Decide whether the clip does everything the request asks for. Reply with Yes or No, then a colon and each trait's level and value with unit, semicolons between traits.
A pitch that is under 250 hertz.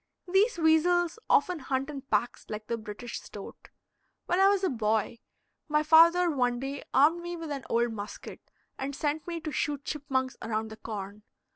No: very high, 280 Hz